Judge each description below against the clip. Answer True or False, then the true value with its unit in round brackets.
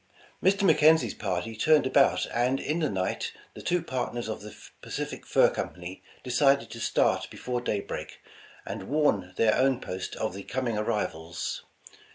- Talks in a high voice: False (120 Hz)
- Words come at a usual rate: True (165 wpm)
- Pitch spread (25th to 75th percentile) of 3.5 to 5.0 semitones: False (5.5 semitones)